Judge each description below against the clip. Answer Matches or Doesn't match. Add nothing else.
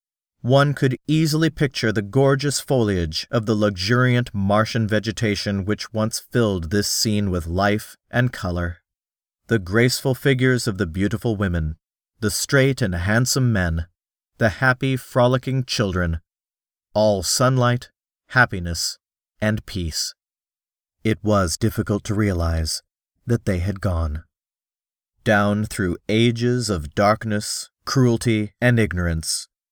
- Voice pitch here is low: Matches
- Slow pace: Matches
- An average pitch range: Matches